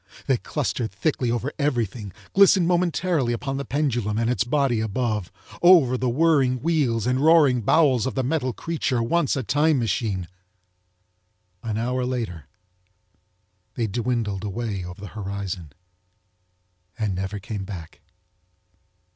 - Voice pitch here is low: Yes, low, 120 Hz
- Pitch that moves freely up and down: No, average, 5.0 semitones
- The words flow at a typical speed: No, slow, 130 wpm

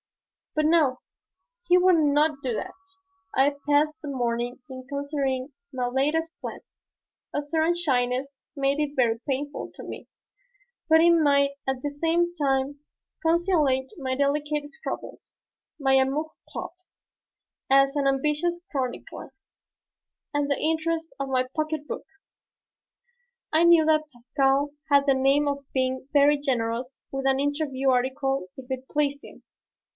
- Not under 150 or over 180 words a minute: No, average, 140 wpm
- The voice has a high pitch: Yes, very high, 280 Hz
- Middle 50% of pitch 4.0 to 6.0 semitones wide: No, narrow, 2.5 semitones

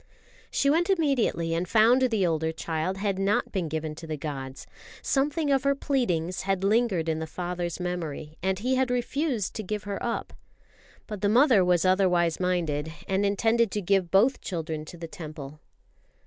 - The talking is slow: No, average, 175 wpm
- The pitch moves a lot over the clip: Yes, wide, 6.0 semitones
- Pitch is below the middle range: No, high, 190 Hz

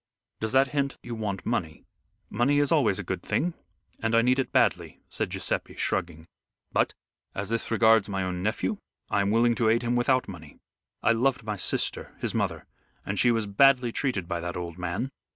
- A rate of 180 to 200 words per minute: Yes, average, 195 wpm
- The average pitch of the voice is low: Yes, low, 115 Hz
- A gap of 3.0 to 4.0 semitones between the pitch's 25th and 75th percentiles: No, average, 4.6 semitones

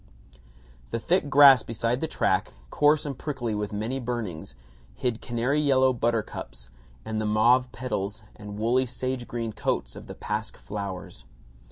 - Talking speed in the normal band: Yes, average, 150 wpm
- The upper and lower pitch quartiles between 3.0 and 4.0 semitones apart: Yes, average, 3.4 semitones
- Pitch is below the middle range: Yes, low, 120 Hz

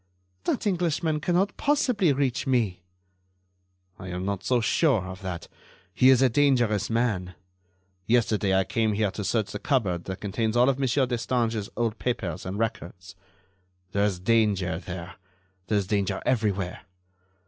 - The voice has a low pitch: Yes, low, 110 Hz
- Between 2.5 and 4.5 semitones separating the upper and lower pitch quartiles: No, average, 5.1 semitones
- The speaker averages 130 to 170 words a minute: Yes, average, 150 wpm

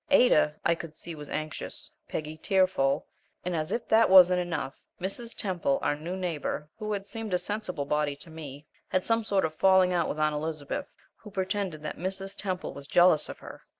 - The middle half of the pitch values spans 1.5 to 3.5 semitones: No, average, 4.0 semitones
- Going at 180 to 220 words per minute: Yes, average, 200 wpm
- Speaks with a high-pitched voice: No, medium, 175 Hz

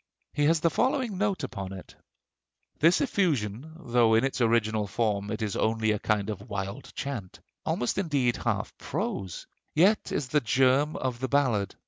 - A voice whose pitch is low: Yes, low, 120 Hz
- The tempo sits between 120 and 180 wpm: Yes, average, 165 wpm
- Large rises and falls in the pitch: Yes, wide, 5.9 semitones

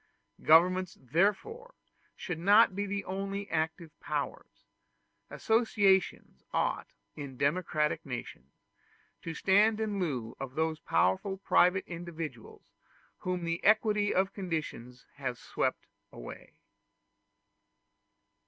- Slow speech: Yes, slow, 100 wpm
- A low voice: No, medium, 180 Hz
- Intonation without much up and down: No, average, 4.6 semitones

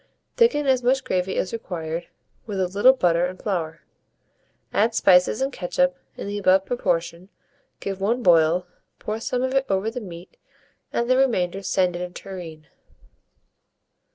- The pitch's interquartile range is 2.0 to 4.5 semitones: No, average, 5.3 semitones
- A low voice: No, high, 195 Hz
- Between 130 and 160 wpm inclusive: Yes, average, 155 wpm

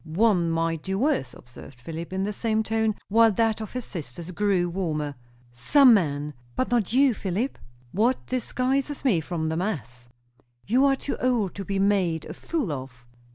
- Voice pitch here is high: Yes, high, 195 Hz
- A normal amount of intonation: No, wide, 6.1 semitones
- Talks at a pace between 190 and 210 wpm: No, average, 175 wpm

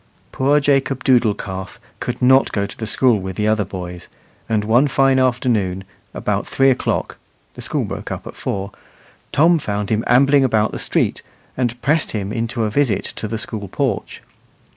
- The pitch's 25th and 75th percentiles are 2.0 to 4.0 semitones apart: No, average, 4.4 semitones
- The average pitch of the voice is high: No, low, 115 Hz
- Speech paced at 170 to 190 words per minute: Yes, average, 180 wpm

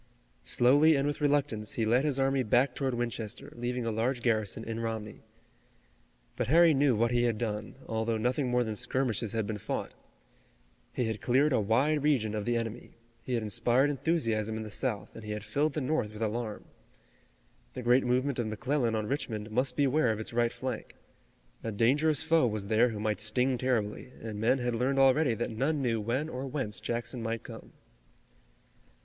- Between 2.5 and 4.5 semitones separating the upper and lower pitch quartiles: Yes, average, 3.4 semitones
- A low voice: Yes, low, 120 Hz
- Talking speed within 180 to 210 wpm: Yes, average, 190 wpm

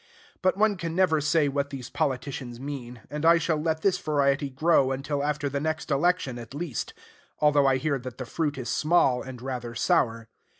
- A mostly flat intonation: No, average, 3.4 semitones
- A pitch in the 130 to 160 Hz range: Yes, medium, 140 Hz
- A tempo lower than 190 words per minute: No, average, 195 wpm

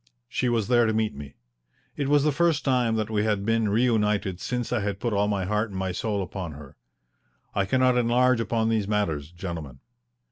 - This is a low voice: Yes, low, 110 Hz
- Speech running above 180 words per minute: Yes, fast, 205 wpm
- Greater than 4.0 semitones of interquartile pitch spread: No, average, 3.7 semitones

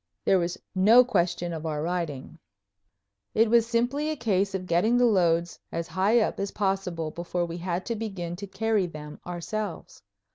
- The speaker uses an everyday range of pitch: Yes, average, 4.2 semitones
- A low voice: No, medium, 185 Hz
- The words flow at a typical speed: Yes, average, 175 wpm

